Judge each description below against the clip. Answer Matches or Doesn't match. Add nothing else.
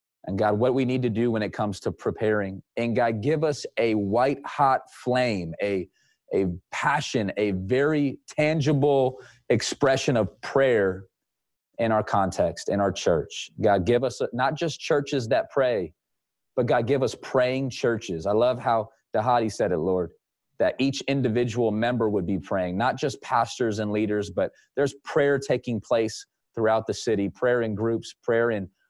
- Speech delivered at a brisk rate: Doesn't match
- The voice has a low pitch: Matches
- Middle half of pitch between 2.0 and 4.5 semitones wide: Matches